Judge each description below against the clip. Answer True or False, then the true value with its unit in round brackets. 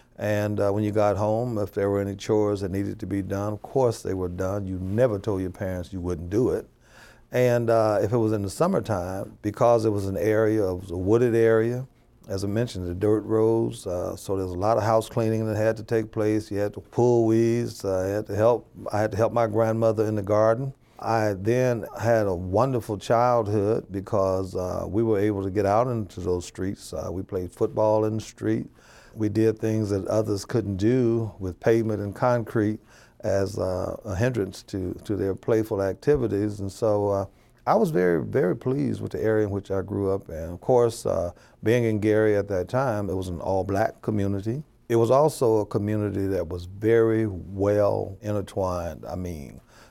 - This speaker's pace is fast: True (210 wpm)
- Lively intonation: False (2.6 semitones)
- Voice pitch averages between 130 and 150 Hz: False (105 Hz)